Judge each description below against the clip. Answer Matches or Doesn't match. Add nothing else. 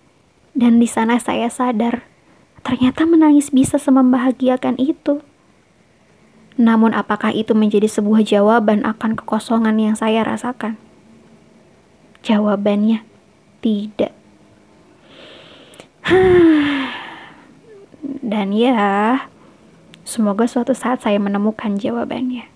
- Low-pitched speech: Doesn't match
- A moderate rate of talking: Doesn't match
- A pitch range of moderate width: Matches